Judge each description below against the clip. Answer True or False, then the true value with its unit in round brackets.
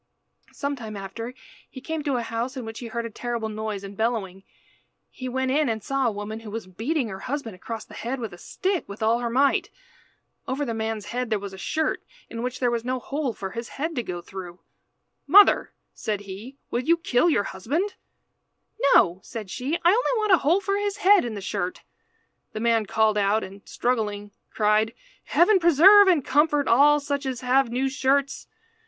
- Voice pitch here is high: True (240 Hz)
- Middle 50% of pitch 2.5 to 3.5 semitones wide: False (4.7 semitones)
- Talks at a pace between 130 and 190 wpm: False (205 wpm)